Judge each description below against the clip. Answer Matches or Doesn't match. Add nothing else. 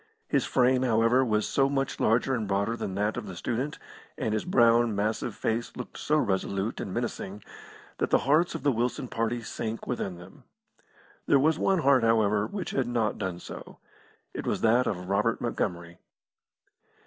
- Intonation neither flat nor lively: Matches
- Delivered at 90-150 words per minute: Doesn't match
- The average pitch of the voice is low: Matches